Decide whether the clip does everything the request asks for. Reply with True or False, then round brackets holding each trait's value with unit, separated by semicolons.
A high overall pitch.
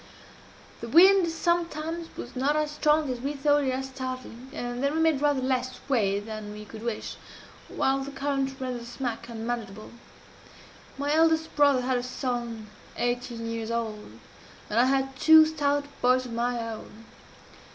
True (255 Hz)